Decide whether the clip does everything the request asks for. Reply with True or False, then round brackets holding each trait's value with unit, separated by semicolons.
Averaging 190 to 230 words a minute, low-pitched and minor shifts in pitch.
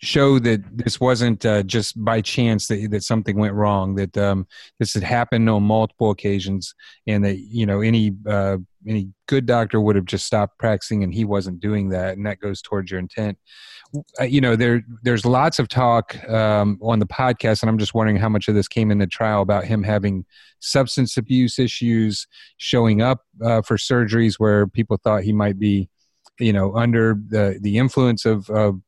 True (195 wpm; 110 Hz; 2.3 semitones)